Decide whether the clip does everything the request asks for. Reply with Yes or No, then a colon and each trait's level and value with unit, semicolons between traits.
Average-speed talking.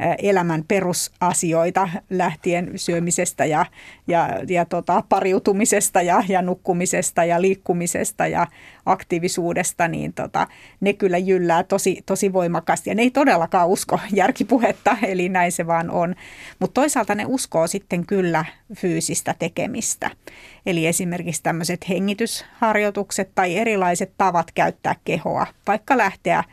Yes: average, 120 wpm